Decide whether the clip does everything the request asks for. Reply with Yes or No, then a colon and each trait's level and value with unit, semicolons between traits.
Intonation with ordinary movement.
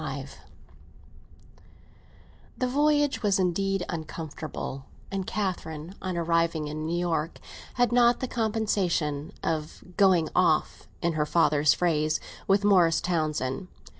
Yes: average, 4.1 semitones